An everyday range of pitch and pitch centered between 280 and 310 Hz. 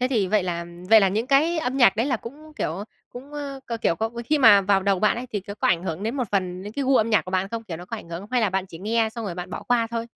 No: average, 4.6 semitones; high, 220 Hz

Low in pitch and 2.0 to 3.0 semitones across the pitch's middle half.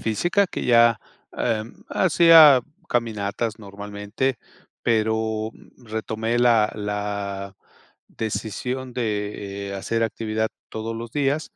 Yes: low, 110 Hz; average, 2.7 semitones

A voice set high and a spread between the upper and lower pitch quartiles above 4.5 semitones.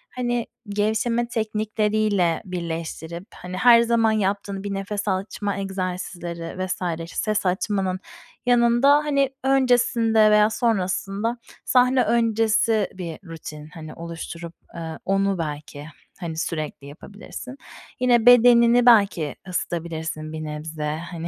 Yes: high, 195 Hz; wide, 5.5 semitones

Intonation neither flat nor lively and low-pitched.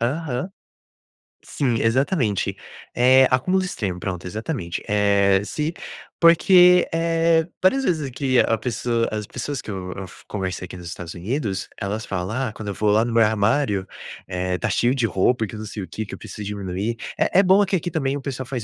No: wide, 6.4 semitones; low, 115 Hz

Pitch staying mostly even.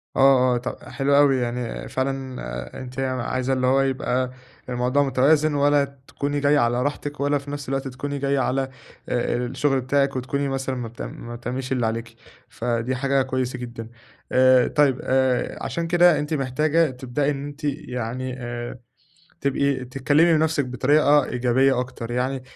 Yes: narrow, 2.2 semitones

